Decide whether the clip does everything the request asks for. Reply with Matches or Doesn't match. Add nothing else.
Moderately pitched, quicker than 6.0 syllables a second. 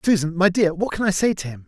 Matches